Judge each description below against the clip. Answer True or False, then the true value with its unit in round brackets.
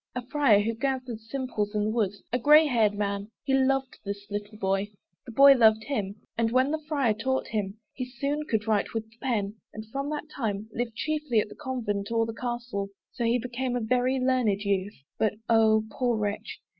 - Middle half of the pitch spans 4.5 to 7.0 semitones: False (3.8 semitones)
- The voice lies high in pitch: True (230 Hz)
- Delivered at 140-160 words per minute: False (205 wpm)